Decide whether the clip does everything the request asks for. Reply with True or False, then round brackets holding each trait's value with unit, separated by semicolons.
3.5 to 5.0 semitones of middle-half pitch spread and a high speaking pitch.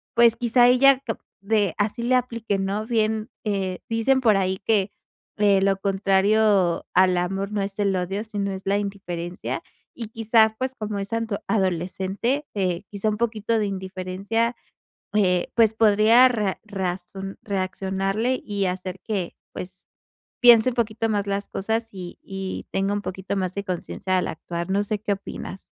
False (2.7 semitones; 200 Hz)